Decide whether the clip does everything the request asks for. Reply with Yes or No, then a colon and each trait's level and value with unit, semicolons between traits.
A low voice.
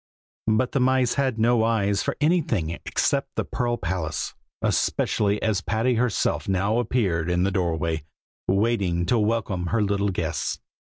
Yes: low, 105 Hz